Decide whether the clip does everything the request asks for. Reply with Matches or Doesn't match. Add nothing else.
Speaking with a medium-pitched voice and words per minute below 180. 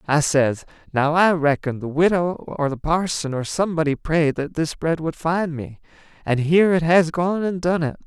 Doesn't match